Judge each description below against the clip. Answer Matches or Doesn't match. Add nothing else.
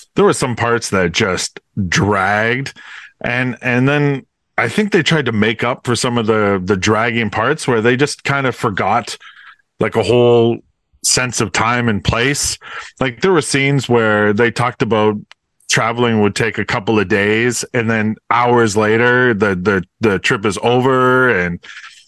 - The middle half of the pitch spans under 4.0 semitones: Matches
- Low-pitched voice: Matches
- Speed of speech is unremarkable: Matches